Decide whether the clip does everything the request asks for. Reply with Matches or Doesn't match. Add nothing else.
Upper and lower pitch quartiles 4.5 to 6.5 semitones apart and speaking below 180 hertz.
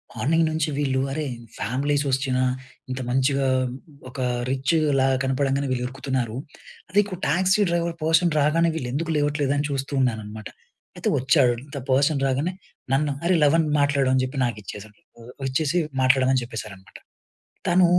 Doesn't match